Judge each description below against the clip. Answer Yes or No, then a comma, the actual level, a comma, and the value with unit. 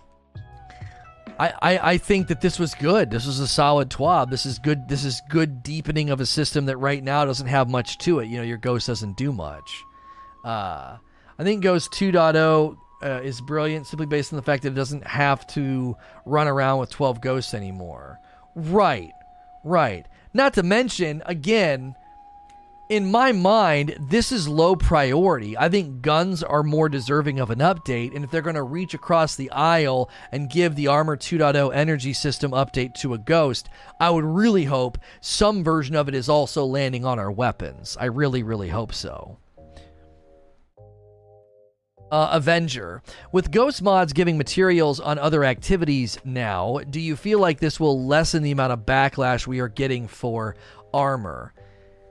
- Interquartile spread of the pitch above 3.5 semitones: Yes, average, 4.9 semitones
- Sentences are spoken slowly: No, average, 170 wpm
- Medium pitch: Yes, medium, 145 Hz